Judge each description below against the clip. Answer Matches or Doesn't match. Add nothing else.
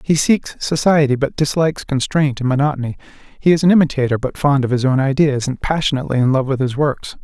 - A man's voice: Matches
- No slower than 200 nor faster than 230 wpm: Matches